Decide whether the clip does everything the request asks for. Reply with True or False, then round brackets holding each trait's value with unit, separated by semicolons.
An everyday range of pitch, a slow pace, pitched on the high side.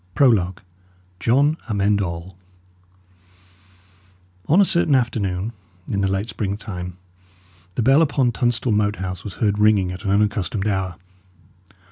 False (3.8 semitones; 125 wpm; 105 Hz)